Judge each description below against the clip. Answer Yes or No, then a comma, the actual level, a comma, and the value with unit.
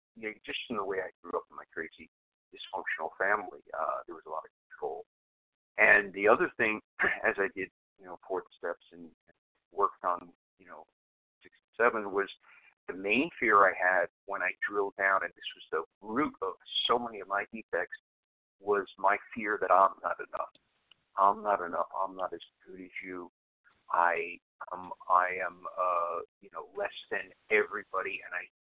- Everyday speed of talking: Yes, average, 185 wpm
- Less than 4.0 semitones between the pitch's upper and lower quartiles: Yes, average, 2.9 semitones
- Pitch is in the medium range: No, very low, 95 Hz